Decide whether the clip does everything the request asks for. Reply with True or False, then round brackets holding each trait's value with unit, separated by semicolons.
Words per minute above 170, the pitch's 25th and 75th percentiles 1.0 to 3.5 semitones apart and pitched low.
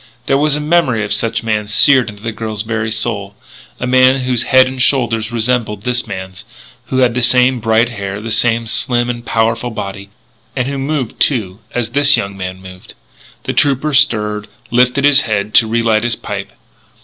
True (190 wpm; 3.1 semitones; 115 Hz)